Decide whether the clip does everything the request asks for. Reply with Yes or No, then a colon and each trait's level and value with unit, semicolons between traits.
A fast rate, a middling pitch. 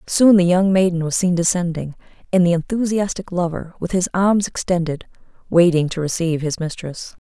No: average, 165 wpm; medium, 175 Hz